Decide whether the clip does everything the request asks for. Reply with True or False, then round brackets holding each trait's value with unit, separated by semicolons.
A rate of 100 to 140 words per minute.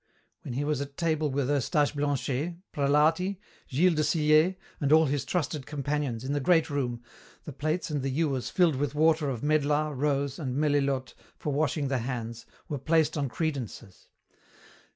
False (165 wpm)